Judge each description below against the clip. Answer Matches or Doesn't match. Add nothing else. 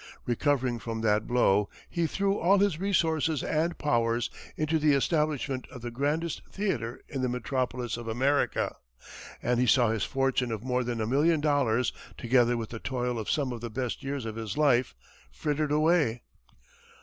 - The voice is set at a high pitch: Doesn't match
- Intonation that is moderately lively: Matches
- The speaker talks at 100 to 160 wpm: Doesn't match